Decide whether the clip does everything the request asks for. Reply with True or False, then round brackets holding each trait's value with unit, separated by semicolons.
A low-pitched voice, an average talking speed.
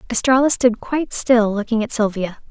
False (230 Hz; 170 wpm)